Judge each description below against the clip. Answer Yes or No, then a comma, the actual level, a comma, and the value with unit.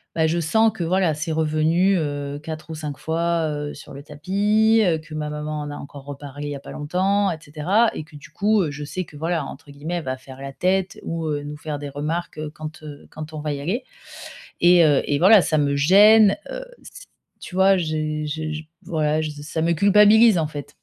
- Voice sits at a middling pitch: Yes, medium, 155 Hz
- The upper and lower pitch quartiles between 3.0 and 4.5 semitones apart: Yes, average, 3.4 semitones